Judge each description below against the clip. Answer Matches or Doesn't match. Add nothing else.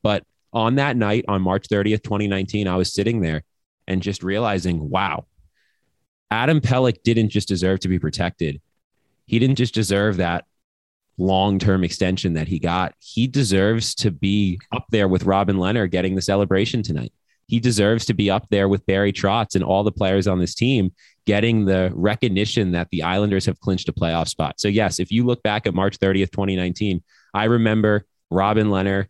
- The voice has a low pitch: Matches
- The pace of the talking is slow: Doesn't match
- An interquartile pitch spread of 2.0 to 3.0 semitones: Matches